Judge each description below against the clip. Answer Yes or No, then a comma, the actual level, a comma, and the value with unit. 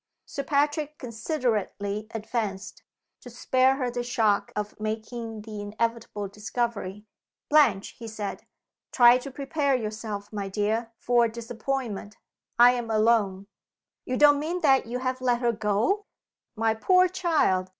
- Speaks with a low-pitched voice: No, high, 230 Hz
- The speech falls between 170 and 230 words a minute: No, average, 140 wpm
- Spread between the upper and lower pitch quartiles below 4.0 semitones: Yes, average, 3.5 semitones